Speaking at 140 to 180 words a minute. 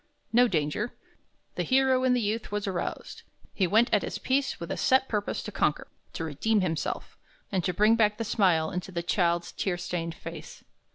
No: average, 190 wpm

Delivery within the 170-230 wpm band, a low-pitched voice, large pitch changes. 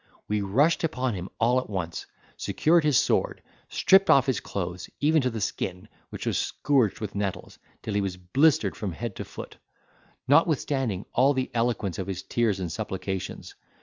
Yes: average, 175 wpm; low, 110 Hz; wide, 5.8 semitones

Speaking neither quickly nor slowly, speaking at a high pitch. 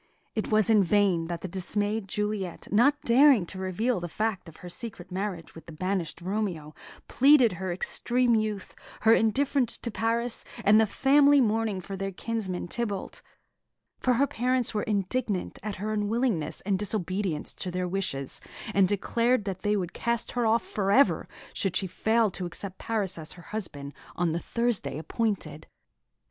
Yes: average, 170 wpm; high, 205 Hz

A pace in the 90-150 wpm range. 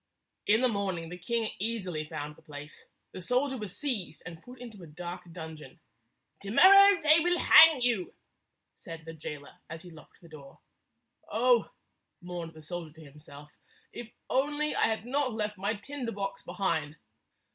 No: average, 170 wpm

